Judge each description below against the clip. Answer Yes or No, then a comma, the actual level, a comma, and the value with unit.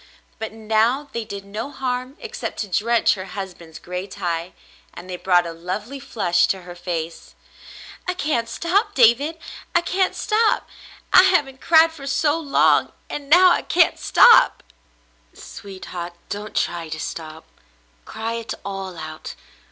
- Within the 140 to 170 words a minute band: Yes, average, 150 wpm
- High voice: Yes, high, 220 Hz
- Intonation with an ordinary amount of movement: No, wide, 8.1 semitones